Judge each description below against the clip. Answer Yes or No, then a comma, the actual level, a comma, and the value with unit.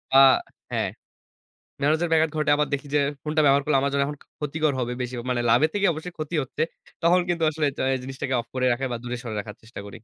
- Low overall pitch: No, medium, 145 Hz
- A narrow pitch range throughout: No, average, 3.6 semitones